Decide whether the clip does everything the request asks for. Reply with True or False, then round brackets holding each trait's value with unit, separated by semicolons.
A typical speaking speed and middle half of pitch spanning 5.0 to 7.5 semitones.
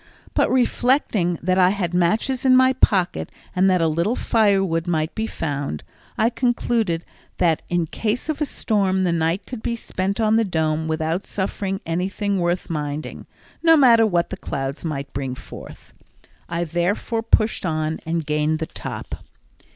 True (165 wpm; 5.4 semitones)